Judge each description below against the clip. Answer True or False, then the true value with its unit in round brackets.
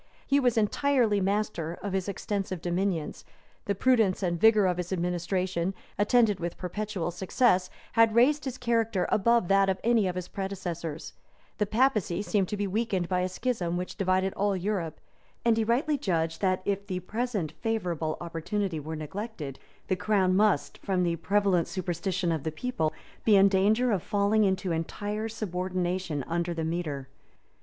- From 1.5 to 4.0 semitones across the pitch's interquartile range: True (3.5 semitones)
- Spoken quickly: False (165 wpm)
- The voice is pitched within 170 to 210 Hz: True (190 Hz)